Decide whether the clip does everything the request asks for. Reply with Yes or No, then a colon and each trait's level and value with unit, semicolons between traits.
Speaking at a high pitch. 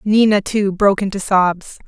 Yes: high, 200 Hz